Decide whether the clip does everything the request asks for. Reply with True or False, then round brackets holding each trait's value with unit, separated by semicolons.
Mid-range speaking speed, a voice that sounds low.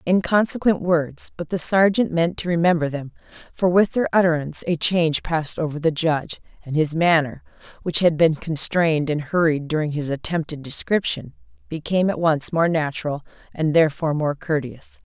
False (165 wpm; 160 Hz)